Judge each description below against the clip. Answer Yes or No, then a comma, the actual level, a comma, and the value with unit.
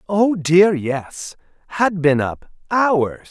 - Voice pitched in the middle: Yes, medium, 170 Hz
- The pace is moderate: No, slow, 90 wpm